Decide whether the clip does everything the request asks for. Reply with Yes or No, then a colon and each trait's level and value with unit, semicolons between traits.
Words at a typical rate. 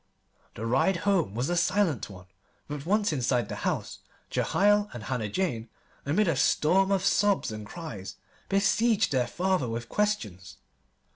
Yes: average, 150 wpm